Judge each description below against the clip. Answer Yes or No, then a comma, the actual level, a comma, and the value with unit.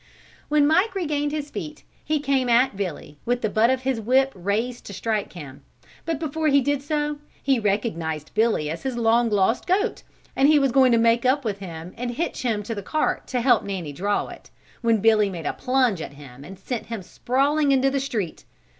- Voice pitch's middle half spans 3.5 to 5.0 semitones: No, wide, 5.5 semitones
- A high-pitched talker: Yes, high, 240 Hz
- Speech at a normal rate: No, fast, 210 wpm